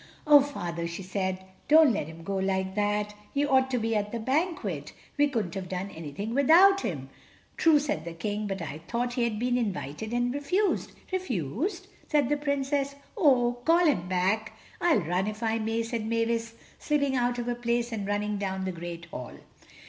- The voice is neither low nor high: No, high, 225 Hz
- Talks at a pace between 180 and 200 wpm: Yes, average, 190 wpm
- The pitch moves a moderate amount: No, wide, 6.4 semitones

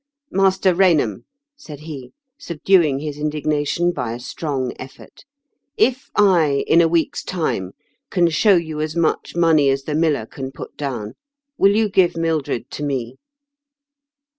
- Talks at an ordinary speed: Yes, average, 155 wpm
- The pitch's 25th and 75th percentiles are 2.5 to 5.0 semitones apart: Yes, average, 4.0 semitones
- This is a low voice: No, medium, 155 Hz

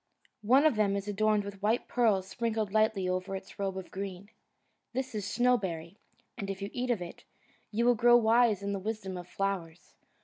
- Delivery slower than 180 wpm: No, average, 195 wpm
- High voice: Yes, high, 205 Hz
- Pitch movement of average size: Yes, average, 3.0 semitones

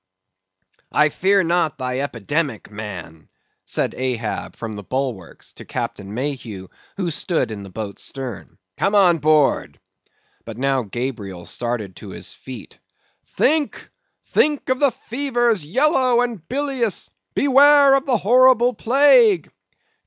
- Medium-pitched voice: Yes, medium, 155 Hz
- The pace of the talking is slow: Yes, slow, 130 wpm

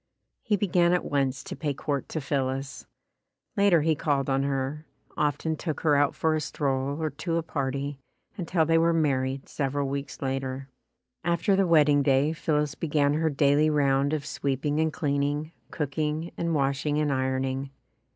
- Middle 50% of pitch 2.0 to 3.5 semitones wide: Yes, narrow, 2.5 semitones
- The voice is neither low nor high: Yes, medium, 145 Hz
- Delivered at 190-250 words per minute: No, average, 165 wpm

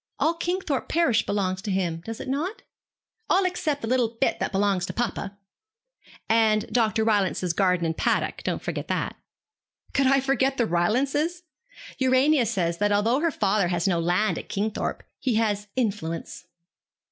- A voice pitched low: No, high, 220 Hz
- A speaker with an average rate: Yes, average, 160 wpm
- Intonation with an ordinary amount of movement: No, wide, 5.7 semitones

